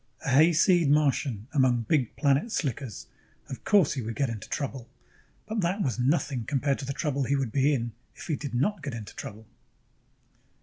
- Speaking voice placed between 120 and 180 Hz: Yes, medium, 140 Hz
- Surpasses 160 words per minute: Yes, average, 190 wpm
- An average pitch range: Yes, average, 3.7 semitones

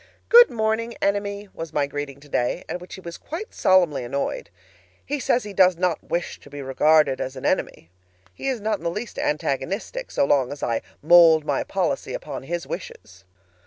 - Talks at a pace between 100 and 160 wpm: No, average, 190 wpm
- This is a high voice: No, medium, 170 Hz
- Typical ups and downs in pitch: No, wide, 6.4 semitones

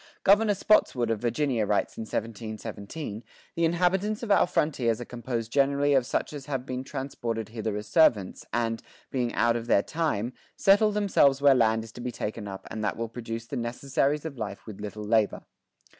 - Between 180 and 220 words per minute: Yes, average, 190 wpm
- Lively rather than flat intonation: No, average, 4.5 semitones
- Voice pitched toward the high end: No, low, 120 Hz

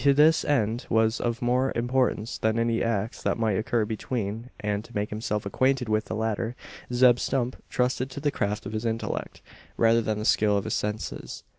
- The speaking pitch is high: No, low, 115 Hz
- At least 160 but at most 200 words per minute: Yes, average, 190 wpm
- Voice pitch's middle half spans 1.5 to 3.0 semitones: Yes, narrow, 2.5 semitones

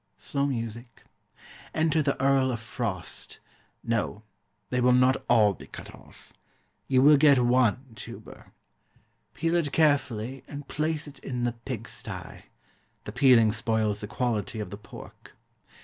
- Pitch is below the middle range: Yes, low, 125 Hz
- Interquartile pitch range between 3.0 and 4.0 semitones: Yes, average, 3.5 semitones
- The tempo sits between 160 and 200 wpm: No, average, 145 wpm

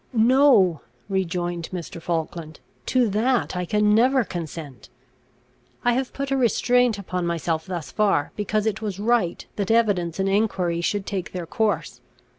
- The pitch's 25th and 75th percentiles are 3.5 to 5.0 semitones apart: Yes, average, 4.5 semitones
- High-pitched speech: Yes, high, 195 Hz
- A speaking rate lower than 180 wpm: Yes, average, 150 wpm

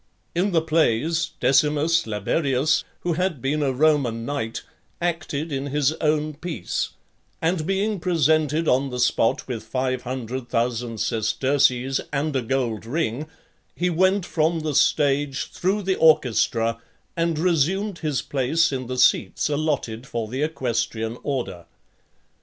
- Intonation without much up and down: No, average, 4.5 semitones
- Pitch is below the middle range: No, medium, 145 Hz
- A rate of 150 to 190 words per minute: No, average, 140 wpm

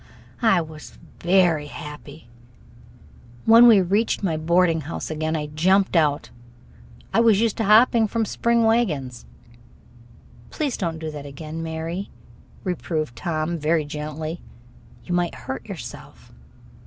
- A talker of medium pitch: Yes, medium, 165 Hz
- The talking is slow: Yes, slow, 130 wpm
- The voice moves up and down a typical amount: Yes, average, 4.5 semitones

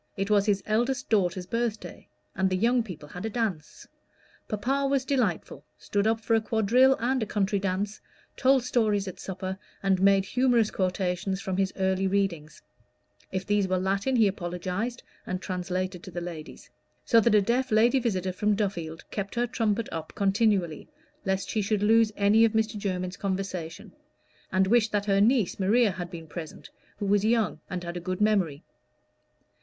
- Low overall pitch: No, high, 200 Hz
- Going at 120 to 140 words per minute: No, average, 175 wpm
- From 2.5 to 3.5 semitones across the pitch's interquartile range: Yes, average, 3.2 semitones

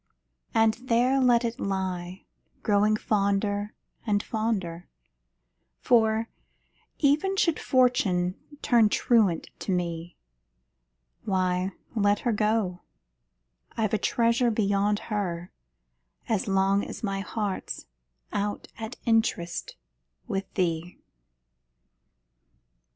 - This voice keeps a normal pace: No, slow, 95 wpm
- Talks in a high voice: Yes, high, 205 Hz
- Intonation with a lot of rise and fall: No, average, 3.1 semitones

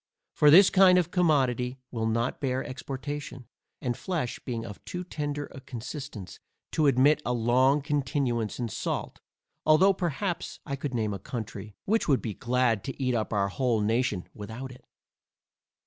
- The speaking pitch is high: No, low, 130 Hz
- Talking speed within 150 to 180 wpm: Yes, average, 165 wpm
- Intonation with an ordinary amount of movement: Yes, average, 4.1 semitones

